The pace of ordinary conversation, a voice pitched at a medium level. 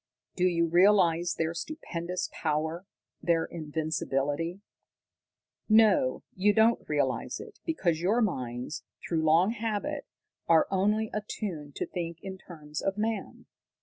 No: slow, 120 wpm; medium, 175 Hz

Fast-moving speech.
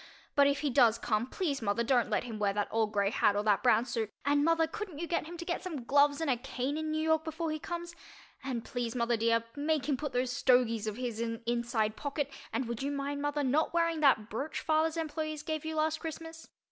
Yes: fast, 245 wpm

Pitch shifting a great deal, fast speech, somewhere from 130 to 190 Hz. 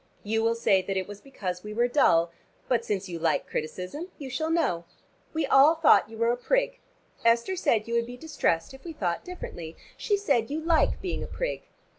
No: wide, 8.3 semitones; fast, 210 wpm; high, 235 Hz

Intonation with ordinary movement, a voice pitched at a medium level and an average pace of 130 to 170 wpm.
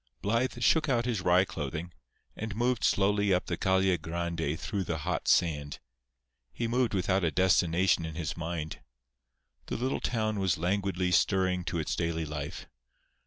No: average, 3.6 semitones; very low, 90 Hz; average, 160 wpm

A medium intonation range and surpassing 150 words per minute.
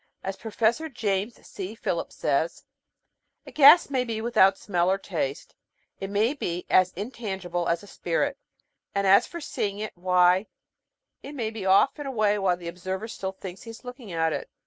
Yes: average, 4.0 semitones; average, 180 wpm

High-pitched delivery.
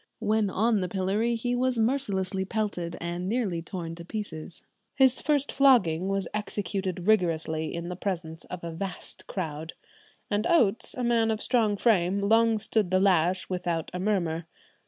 Yes: high, 195 Hz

